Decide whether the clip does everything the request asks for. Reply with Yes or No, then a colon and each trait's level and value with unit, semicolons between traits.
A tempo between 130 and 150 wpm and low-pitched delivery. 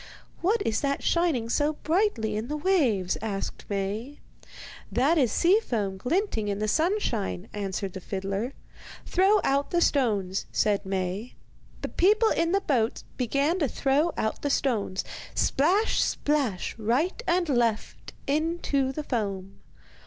No: average, 140 wpm; very high, 260 Hz